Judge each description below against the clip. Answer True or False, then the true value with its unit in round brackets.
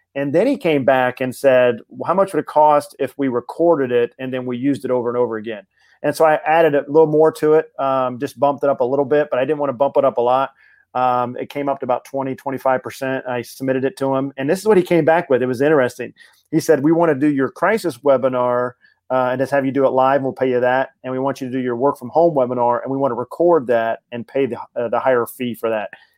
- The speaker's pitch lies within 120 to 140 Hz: True (135 Hz)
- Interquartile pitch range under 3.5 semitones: True (2.8 semitones)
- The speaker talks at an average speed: False (285 wpm)